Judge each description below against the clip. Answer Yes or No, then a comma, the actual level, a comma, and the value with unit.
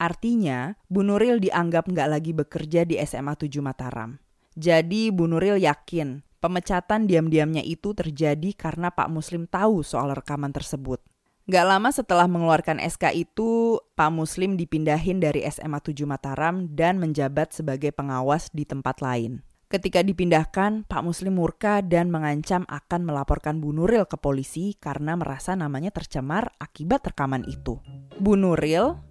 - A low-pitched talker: No, medium, 165 Hz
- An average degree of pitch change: Yes, average, 3.8 semitones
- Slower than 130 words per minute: No, fast, 140 wpm